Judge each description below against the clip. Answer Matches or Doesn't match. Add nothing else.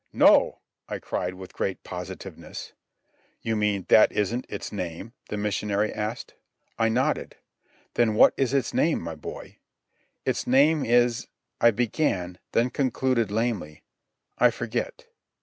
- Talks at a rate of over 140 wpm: Doesn't match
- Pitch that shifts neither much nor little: Matches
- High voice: Doesn't match